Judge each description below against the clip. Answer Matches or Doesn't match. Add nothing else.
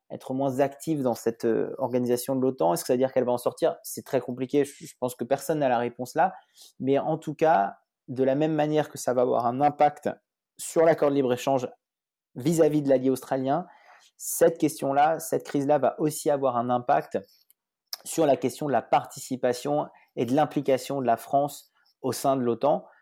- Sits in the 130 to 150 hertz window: Matches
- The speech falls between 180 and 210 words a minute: Matches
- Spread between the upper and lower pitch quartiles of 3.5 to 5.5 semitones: Doesn't match